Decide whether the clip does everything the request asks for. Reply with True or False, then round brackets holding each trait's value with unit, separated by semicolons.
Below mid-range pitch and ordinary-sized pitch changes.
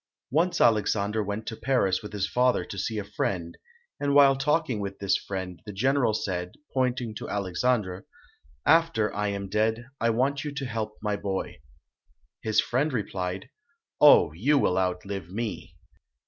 True (105 Hz; 4.6 semitones)